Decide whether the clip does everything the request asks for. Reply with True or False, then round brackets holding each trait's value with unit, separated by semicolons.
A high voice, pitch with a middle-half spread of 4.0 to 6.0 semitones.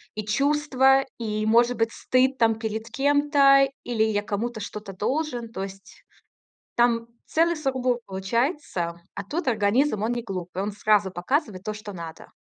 True (230 Hz; 4.6 semitones)